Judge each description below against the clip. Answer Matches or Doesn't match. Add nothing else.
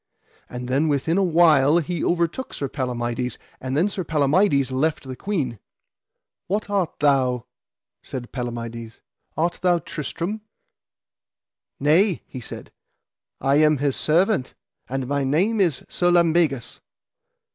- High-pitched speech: Doesn't match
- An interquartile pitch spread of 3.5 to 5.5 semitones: Matches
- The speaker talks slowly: Matches